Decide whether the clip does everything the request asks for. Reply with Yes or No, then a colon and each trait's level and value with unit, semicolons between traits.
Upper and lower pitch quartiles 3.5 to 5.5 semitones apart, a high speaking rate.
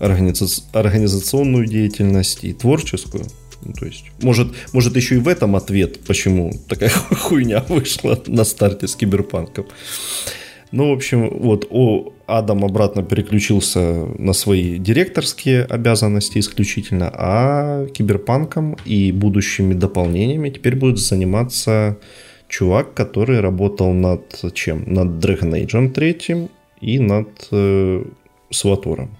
No: average, 4.3 semitones; average, 115 wpm